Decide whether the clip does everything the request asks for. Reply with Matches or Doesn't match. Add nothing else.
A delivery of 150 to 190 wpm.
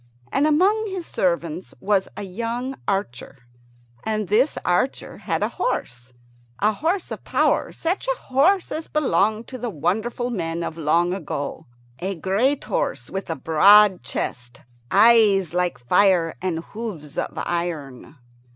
Doesn't match